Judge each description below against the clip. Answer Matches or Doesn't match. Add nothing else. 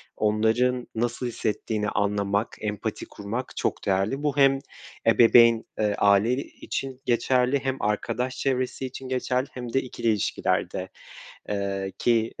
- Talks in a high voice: Doesn't match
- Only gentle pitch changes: Doesn't match